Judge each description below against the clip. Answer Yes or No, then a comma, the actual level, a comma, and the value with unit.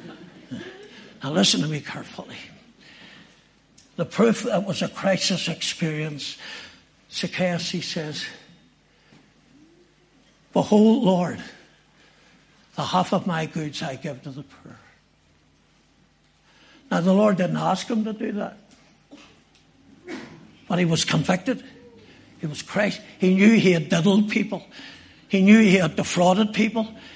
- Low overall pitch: No, medium, 185 Hz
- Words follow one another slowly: Yes, slow, 120 wpm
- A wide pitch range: No, average, 4.3 semitones